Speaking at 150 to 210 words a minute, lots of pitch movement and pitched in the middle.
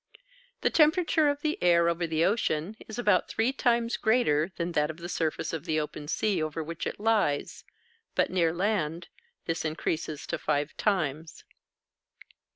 Yes: average, 160 wpm; wide, 5.7 semitones; medium, 170 Hz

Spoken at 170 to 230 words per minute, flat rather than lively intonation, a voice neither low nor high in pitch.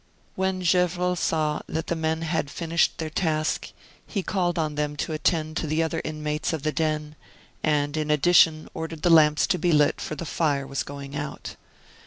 Yes: average, 190 wpm; narrow, 1.8 semitones; medium, 155 Hz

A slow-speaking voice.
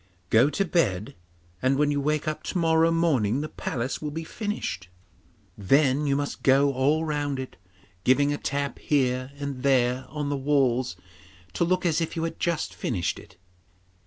No: average, 175 wpm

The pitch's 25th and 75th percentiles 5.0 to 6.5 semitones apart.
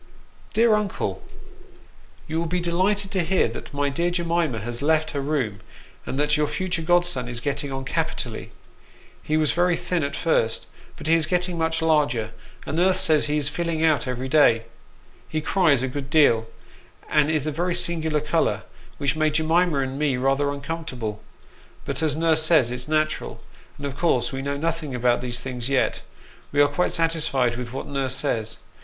No: average, 3.8 semitones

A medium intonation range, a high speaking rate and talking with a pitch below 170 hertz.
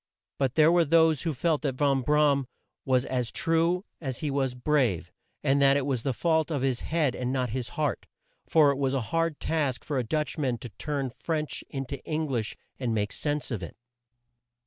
Yes: average, 3.3 semitones; fast, 215 wpm; medium, 140 Hz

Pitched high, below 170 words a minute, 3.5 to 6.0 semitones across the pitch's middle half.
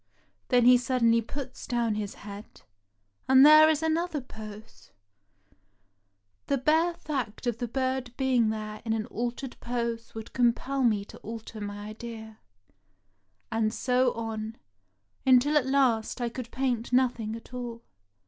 No: high, 240 Hz; average, 145 wpm; average, 2.8 semitones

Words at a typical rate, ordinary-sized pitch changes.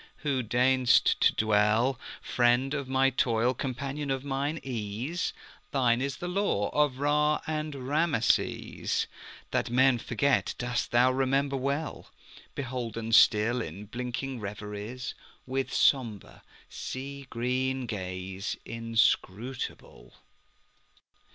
No: slow, 95 wpm; average, 3.1 semitones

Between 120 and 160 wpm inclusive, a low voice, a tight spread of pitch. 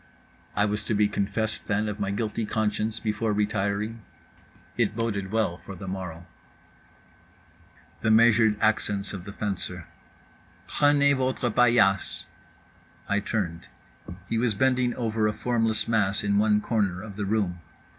Yes: average, 140 wpm; low, 105 Hz; narrow, 2.0 semitones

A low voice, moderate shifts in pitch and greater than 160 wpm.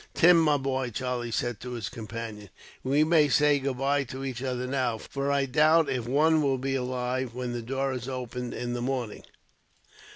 No: low, 130 Hz; narrow, 2.2 semitones; average, 190 wpm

